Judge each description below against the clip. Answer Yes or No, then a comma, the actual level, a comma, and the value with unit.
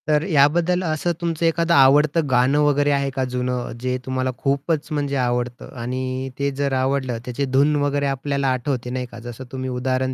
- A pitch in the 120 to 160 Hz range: Yes, low, 135 Hz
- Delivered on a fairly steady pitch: Yes, narrow, 2.3 semitones